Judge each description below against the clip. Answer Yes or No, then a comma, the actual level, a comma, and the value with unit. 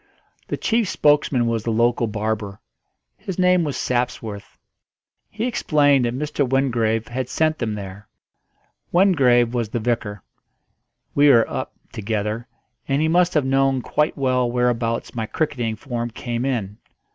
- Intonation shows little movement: No, average, 4.2 semitones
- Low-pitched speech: Yes, low, 120 Hz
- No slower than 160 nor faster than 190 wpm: No, average, 145 wpm